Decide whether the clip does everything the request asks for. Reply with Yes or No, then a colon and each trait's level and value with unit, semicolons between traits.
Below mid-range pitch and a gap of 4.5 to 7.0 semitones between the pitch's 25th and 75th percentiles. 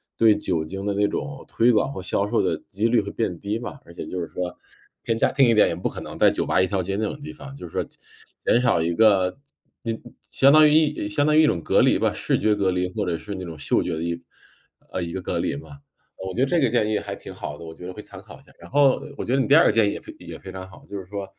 Yes: low, 105 Hz; average, 5.2 semitones